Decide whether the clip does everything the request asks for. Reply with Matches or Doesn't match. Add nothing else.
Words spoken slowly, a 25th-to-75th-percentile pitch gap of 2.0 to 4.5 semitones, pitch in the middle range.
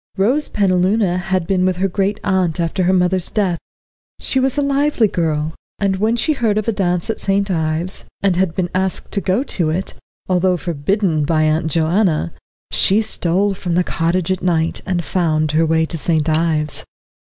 Doesn't match